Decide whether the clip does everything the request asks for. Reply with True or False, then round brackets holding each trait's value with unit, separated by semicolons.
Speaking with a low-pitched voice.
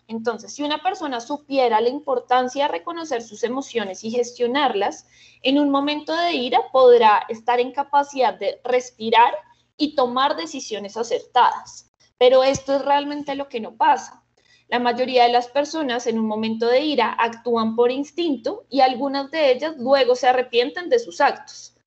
False (260 Hz)